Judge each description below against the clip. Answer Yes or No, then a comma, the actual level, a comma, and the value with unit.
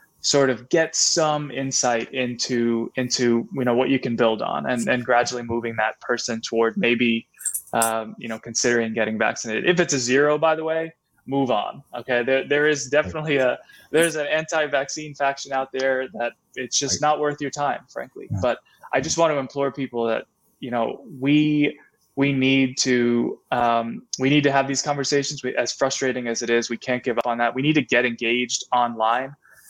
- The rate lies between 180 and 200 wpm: Yes, average, 195 wpm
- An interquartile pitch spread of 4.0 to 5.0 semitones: No, average, 3.3 semitones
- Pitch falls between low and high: No, low, 130 Hz